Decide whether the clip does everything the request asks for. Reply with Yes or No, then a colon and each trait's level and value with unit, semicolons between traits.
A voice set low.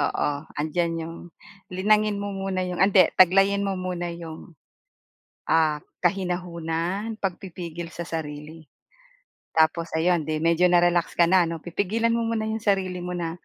No: medium, 175 Hz